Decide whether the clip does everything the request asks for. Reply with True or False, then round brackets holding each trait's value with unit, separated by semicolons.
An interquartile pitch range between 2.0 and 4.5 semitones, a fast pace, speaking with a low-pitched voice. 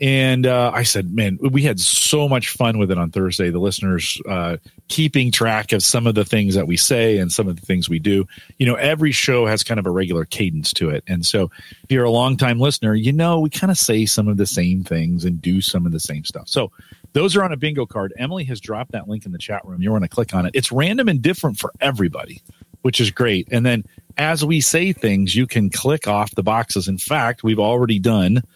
False (5.0 semitones; 250 wpm; 110 Hz)